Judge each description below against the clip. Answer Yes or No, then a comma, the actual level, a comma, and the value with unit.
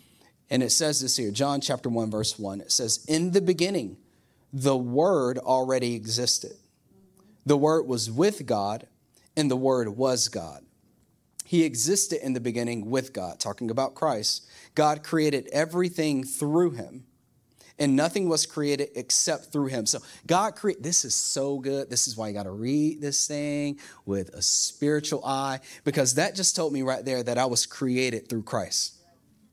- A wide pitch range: No, average, 3.8 semitones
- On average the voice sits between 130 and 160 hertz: Yes, low, 135 Hz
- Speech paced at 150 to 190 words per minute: Yes, average, 170 wpm